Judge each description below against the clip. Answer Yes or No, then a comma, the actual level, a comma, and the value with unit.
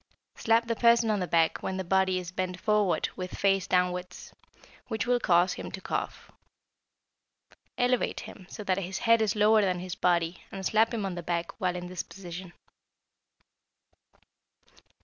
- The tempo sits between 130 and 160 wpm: No, average, 170 wpm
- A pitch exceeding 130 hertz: Yes, high, 190 Hz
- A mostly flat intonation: No, average, 3.2 semitones